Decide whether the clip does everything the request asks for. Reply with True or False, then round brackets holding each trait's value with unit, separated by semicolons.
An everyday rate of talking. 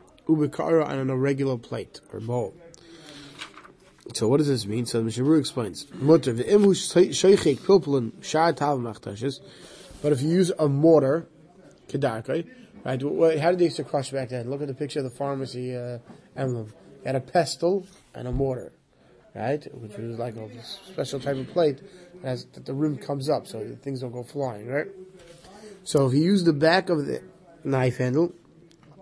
True (165 wpm)